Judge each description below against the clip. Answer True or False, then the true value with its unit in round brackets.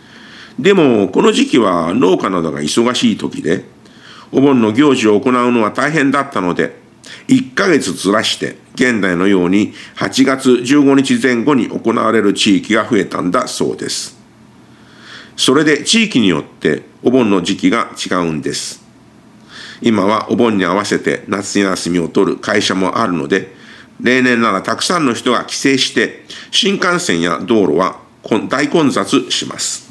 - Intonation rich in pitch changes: True (6.5 semitones)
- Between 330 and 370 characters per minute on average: False (275 characters per minute)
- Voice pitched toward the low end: True (125 Hz)